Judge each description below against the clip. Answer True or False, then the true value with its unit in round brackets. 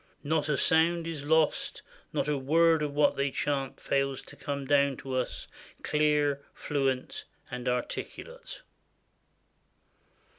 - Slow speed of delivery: True (125 wpm)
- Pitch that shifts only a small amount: True (2.3 semitones)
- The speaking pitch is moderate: True (145 Hz)